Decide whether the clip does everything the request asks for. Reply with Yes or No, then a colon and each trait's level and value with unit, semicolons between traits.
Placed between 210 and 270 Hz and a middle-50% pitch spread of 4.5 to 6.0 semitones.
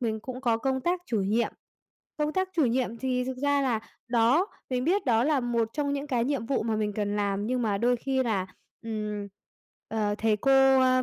No: high, 245 Hz; average, 3.5 semitones